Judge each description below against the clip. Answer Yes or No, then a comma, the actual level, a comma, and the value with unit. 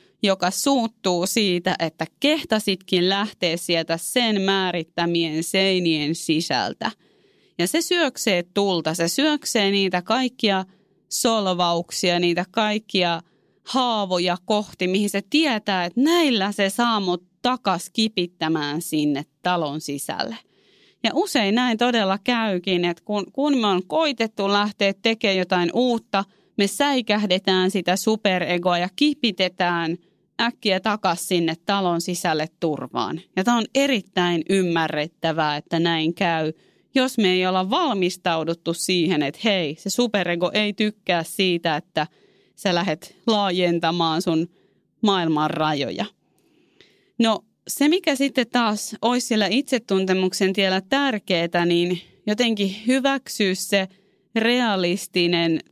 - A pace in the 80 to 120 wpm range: Yes, average, 115 wpm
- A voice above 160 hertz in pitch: Yes, high, 190 Hz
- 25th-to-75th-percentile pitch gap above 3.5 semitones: Yes, average, 4.2 semitones